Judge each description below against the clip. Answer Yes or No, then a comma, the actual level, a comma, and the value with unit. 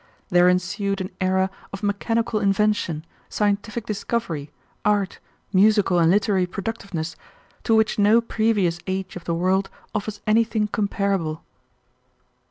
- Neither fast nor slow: No, slow, 120 wpm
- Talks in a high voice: Yes, high, 200 Hz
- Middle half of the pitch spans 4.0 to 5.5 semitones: No, average, 2.7 semitones